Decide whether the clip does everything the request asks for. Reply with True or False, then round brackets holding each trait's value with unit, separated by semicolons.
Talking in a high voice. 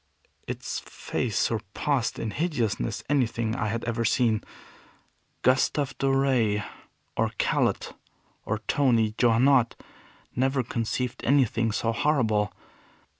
False (120 Hz)